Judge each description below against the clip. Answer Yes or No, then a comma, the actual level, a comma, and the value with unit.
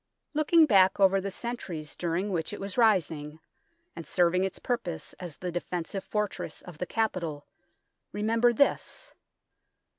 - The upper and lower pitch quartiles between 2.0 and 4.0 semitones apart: No, average, 4.4 semitones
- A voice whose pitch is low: No, high, 190 Hz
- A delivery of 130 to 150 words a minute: Yes, average, 140 wpm